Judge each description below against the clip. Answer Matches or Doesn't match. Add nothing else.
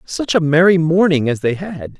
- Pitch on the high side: Doesn't match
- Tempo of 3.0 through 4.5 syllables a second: Doesn't match